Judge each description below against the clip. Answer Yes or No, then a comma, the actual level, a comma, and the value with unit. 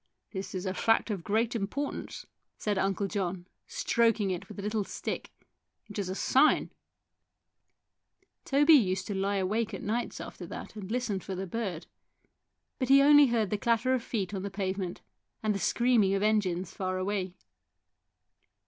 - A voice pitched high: Yes, high, 205 Hz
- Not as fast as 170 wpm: No, average, 175 wpm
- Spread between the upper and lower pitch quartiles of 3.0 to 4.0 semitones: Yes, average, 3.4 semitones